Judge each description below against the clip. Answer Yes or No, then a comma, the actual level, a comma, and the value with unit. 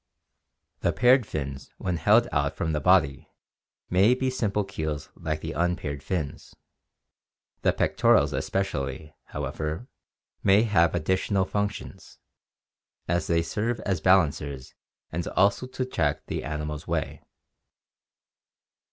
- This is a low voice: Yes, very low, 85 Hz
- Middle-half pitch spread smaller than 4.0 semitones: No, average, 5.1 semitones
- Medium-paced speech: No, slow, 115 wpm